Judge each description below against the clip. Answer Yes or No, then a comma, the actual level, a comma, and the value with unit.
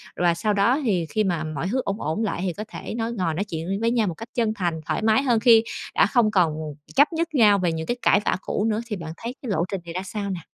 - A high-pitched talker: Yes, high, 205 Hz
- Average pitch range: Yes, average, 4.7 semitones